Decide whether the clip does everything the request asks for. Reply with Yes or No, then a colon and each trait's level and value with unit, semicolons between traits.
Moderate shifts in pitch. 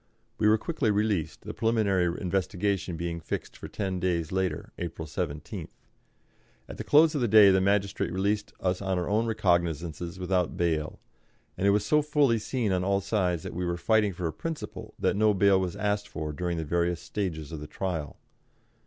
Yes: average, 3.3 semitones